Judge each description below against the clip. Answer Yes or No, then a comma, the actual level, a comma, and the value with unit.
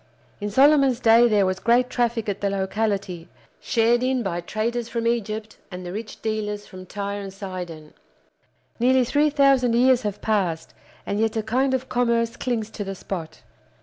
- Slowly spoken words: No, average, 175 wpm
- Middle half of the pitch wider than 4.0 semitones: No, average, 3.5 semitones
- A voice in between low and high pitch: No, high, 220 Hz